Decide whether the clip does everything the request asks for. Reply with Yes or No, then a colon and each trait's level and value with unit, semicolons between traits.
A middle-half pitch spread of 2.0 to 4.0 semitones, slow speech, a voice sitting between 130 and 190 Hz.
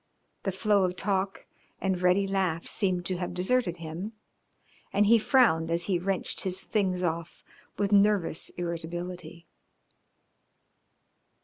Yes: narrow, 2.4 semitones; slow, 125 wpm; medium, 185 Hz